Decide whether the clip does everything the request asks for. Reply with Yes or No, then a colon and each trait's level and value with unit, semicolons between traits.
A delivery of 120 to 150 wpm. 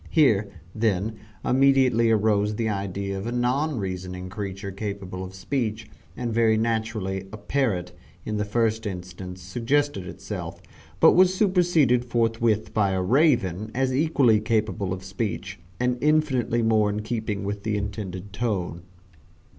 Yes: average, 140 wpm